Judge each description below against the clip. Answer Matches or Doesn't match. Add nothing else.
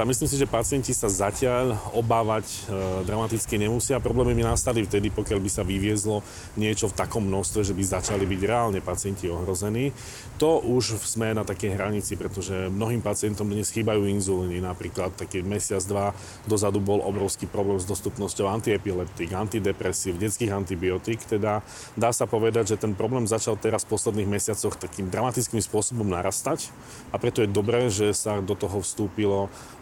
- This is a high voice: Doesn't match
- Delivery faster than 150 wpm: Matches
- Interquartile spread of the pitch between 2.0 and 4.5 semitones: Matches